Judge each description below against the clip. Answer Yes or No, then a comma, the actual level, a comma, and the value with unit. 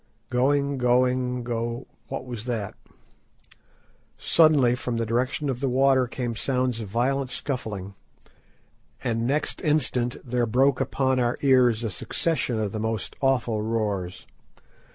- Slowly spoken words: Yes, slow, 130 wpm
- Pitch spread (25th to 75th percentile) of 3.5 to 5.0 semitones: No, narrow, 2.4 semitones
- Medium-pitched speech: No, low, 125 Hz